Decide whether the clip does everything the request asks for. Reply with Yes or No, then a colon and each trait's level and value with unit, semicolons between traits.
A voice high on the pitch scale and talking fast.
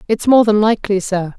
Yes: high, 205 Hz; fast, 215 wpm